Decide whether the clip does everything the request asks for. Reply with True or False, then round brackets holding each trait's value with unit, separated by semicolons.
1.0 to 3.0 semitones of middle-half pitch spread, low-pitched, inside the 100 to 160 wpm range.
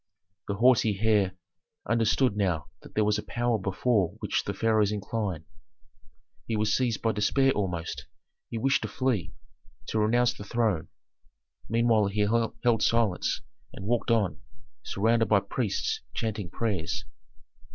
True (2.6 semitones; 110 Hz; 140 wpm)